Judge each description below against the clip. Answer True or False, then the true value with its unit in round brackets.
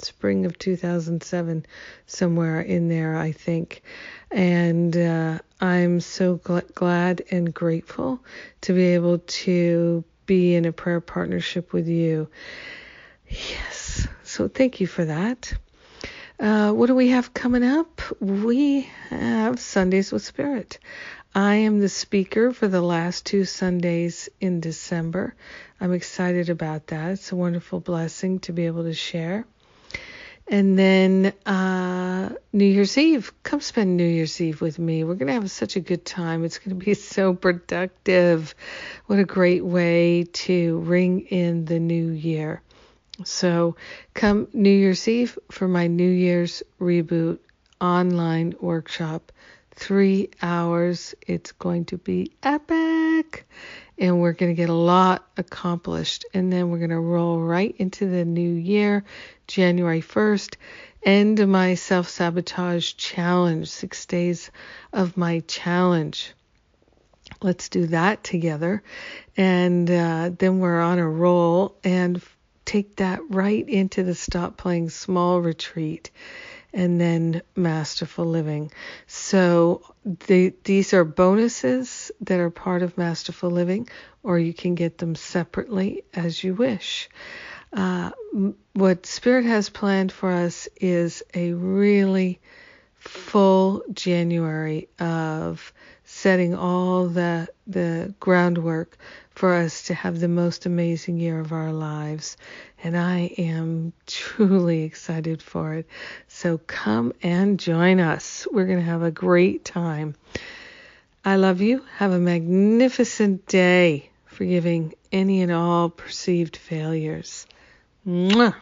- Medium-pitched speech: True (180 Hz)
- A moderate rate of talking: False (130 wpm)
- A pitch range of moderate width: False (2.3 semitones)